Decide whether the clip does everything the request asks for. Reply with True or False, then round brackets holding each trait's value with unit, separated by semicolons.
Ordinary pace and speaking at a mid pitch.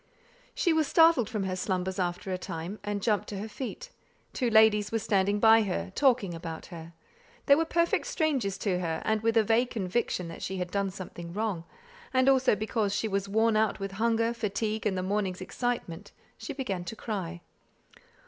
False (190 wpm; 210 Hz)